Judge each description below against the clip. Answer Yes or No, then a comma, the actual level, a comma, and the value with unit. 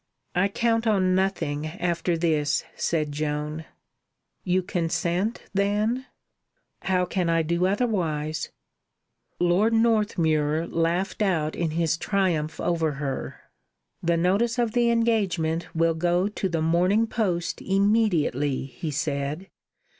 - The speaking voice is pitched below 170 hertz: No, medium, 175 Hz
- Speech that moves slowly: Yes, slow, 115 wpm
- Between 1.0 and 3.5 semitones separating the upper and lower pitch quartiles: No, average, 4.0 semitones